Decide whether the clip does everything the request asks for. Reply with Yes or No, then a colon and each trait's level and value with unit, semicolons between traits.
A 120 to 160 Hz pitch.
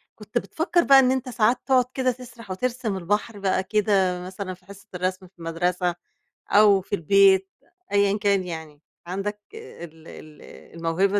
No: high, 195 Hz